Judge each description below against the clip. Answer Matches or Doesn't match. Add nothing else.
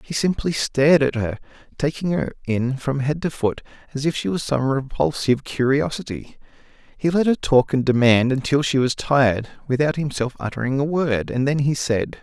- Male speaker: Matches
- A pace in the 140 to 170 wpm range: Doesn't match